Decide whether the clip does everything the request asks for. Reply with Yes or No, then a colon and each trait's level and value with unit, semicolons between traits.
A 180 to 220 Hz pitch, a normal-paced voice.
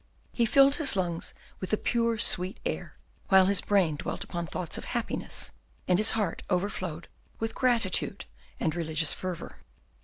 Yes: high, 190 Hz; average, 155 wpm